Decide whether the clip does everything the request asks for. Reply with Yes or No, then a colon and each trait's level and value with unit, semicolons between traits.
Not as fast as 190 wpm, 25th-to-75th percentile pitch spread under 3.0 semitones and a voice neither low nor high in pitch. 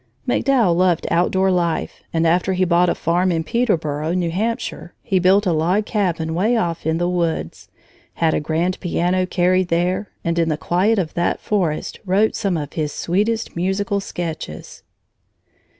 Yes: average, 165 wpm; narrow, 2.4 semitones; medium, 180 Hz